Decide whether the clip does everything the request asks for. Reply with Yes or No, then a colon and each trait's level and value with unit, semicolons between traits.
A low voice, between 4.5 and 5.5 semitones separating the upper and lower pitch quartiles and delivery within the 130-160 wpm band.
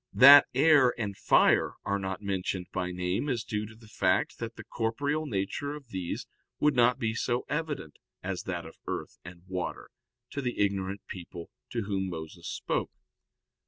No: low, 105 Hz; average, 5.0 semitones; average, 170 wpm